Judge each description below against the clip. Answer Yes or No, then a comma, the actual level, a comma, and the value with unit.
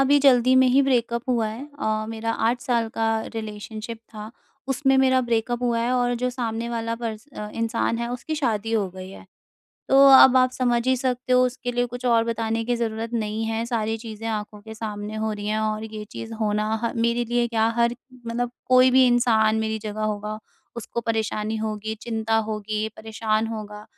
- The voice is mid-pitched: No, high, 225 Hz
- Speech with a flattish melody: Yes, narrow, 2.0 semitones